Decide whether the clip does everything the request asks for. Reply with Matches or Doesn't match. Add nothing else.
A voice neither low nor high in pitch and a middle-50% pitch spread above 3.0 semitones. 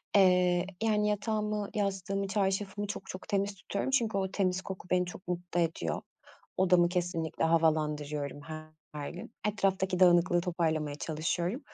Doesn't match